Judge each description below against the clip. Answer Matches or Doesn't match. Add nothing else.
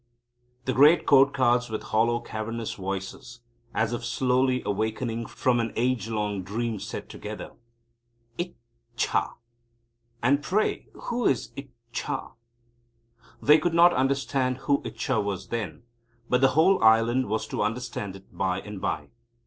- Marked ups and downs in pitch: Doesn't match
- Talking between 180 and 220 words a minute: Doesn't match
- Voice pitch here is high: Doesn't match